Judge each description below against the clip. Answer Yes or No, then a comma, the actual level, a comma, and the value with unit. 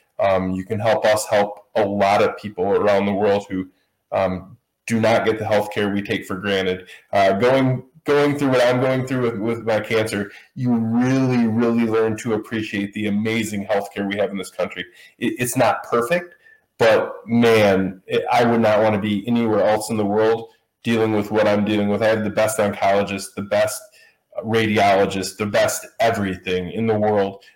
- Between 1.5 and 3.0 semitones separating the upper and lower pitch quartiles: Yes, narrow, 2.5 semitones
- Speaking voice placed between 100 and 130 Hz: Yes, low, 110 Hz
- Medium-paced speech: Yes, average, 195 wpm